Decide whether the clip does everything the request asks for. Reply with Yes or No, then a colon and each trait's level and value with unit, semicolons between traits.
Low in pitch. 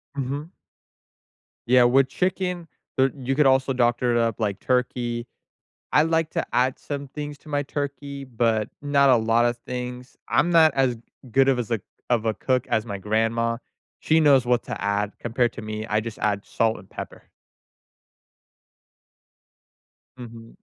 Yes: low, 125 Hz